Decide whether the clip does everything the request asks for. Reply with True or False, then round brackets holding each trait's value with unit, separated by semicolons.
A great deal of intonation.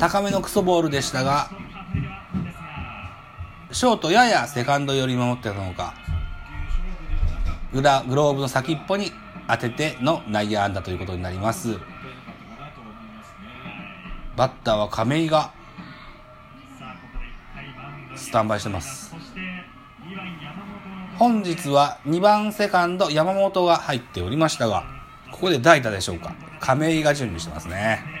True (8.4 semitones)